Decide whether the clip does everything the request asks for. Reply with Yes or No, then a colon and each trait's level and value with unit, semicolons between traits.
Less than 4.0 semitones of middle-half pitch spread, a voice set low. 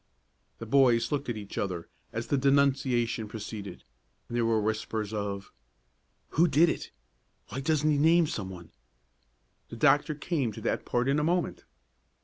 No: average, 5.1 semitones; low, 120 Hz